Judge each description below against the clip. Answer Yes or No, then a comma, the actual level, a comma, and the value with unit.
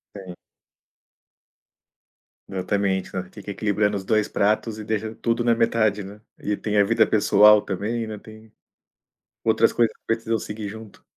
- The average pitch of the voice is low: Yes, low, 105 Hz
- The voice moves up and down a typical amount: No, narrow, 1.6 semitones